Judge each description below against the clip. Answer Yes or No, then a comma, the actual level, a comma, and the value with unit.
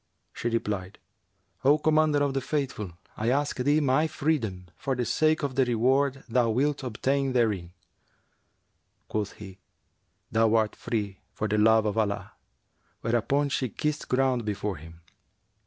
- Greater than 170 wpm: No, average, 150 wpm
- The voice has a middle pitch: No, low, 120 Hz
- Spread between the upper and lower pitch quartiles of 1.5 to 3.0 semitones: No, average, 4.6 semitones